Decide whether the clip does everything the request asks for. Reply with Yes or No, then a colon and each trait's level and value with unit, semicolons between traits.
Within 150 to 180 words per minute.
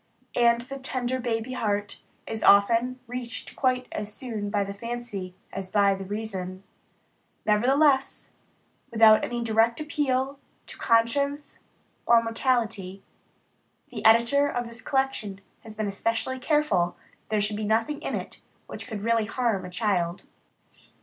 No: average, 140 wpm